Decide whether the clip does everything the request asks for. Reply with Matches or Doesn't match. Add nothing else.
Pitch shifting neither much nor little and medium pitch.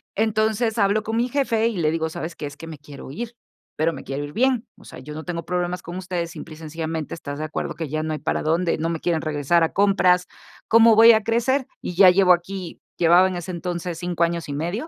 Matches